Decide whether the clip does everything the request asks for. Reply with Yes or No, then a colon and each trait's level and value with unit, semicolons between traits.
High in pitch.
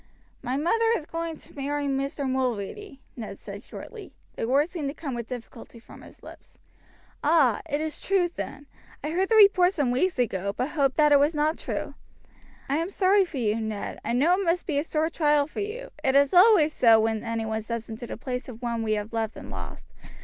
Yes: very high, 280 Hz